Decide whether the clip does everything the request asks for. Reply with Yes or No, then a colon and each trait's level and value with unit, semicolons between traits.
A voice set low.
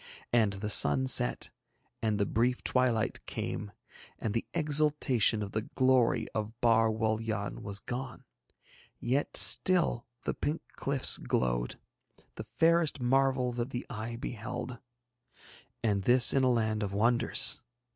Yes: low, 115 Hz